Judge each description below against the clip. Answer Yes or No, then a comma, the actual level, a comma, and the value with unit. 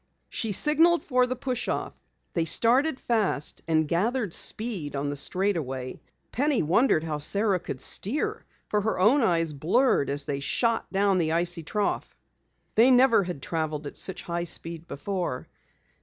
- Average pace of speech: Yes, average, 155 wpm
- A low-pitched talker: No, medium, 185 Hz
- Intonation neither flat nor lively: No, wide, 7.0 semitones